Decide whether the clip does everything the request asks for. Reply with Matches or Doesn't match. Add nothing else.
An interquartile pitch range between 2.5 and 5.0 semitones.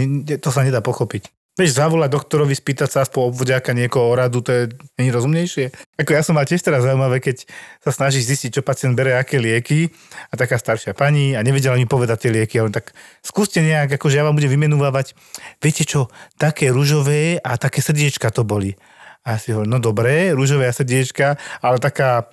Matches